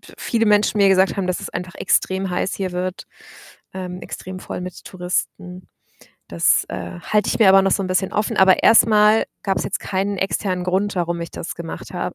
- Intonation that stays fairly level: Yes, narrow, 1.7 semitones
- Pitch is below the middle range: No, medium, 185 Hz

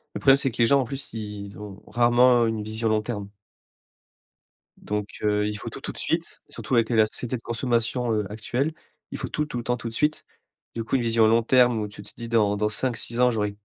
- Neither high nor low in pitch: No, low, 115 Hz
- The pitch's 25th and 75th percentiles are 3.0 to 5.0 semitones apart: No, narrow, 2.5 semitones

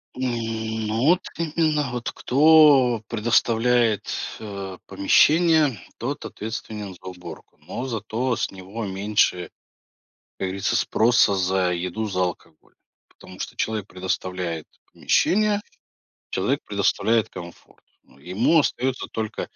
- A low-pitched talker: Yes, low, 110 Hz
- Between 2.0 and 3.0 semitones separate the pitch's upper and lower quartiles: No, average, 4.9 semitones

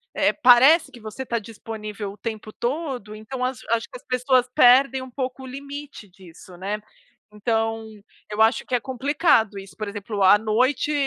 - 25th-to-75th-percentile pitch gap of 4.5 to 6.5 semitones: No, average, 3.6 semitones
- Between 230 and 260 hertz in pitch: Yes, high, 235 Hz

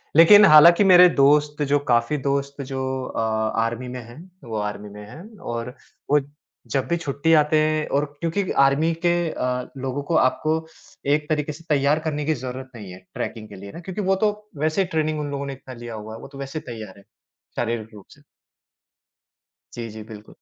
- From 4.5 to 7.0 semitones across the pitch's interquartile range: Yes, average, 4.8 semitones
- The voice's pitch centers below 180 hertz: Yes, medium, 140 Hz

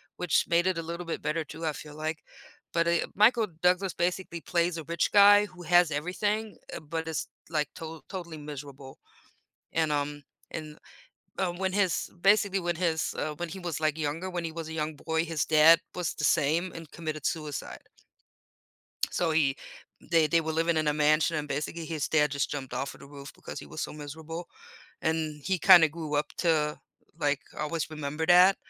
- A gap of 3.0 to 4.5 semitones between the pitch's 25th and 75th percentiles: No, narrow, 2.4 semitones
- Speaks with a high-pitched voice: No, medium, 160 Hz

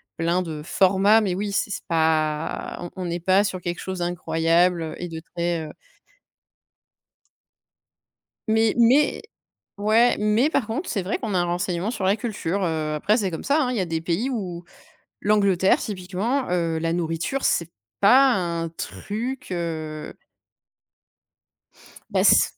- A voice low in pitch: No, medium, 185 Hz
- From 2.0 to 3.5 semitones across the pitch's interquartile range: No, average, 4.2 semitones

